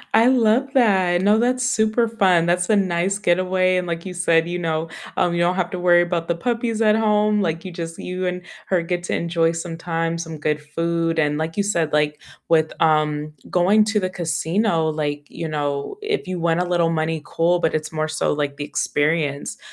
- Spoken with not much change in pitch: No, average, 3.0 semitones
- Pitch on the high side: No, medium, 175 Hz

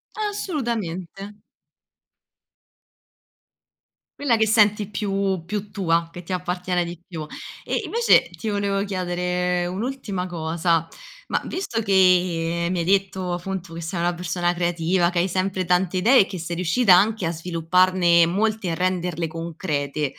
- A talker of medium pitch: Yes, medium, 180 Hz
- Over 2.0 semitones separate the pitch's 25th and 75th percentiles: Yes, narrow, 2.5 semitones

